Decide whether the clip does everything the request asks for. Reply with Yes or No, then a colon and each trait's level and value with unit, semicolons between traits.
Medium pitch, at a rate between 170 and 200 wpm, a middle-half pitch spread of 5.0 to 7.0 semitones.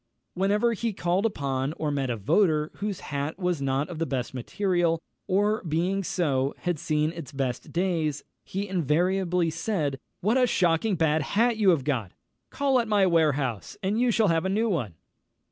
Yes: medium, 170 Hz; average, 180 wpm; average, 5.3 semitones